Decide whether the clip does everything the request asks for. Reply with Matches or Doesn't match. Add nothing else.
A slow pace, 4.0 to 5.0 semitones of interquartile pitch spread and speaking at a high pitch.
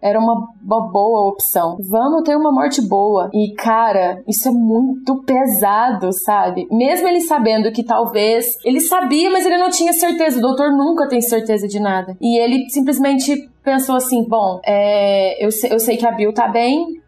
Doesn't match